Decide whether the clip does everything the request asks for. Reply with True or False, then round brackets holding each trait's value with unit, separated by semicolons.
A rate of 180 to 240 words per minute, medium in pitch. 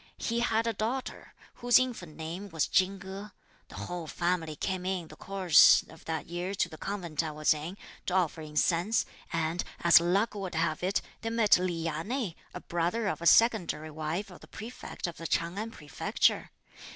True (190 wpm; 180 Hz)